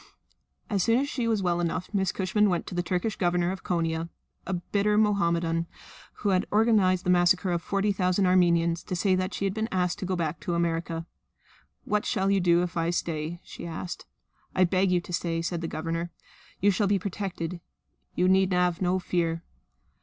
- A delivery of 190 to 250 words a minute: Yes, average, 200 wpm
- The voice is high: No, medium, 180 Hz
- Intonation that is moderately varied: No, narrow, 2.2 semitones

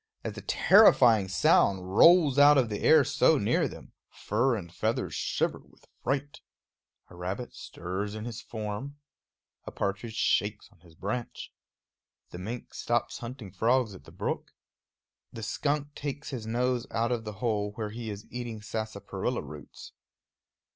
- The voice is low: Yes, low, 110 Hz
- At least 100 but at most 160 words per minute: Yes, average, 155 wpm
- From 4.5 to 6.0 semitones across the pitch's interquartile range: No, average, 3.4 semitones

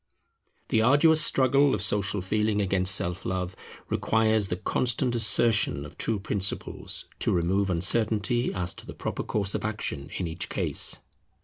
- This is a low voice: Yes, low, 105 Hz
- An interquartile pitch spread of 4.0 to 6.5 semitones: No, average, 3.4 semitones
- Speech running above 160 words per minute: No, average, 150 wpm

